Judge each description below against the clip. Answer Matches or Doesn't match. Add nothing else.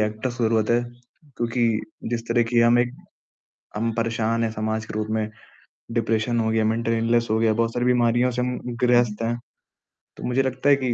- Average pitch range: Doesn't match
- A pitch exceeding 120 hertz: Doesn't match